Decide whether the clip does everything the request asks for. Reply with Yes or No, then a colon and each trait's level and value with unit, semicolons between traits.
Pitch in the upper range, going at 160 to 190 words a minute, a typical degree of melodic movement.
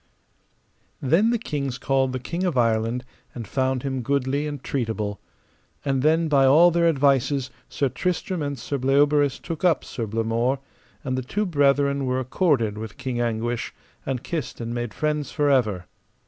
No: low, 135 Hz; average, 165 wpm; average, 3.4 semitones